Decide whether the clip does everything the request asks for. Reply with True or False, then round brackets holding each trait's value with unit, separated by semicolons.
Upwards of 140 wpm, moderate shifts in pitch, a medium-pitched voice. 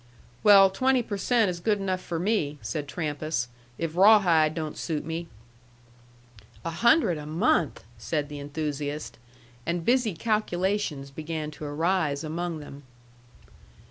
False (135 wpm; 4.5 semitones; 165 Hz)